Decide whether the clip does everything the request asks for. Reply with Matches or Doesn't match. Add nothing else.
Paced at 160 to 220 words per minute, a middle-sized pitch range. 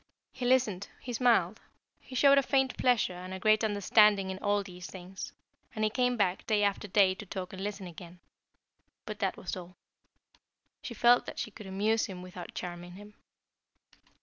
Matches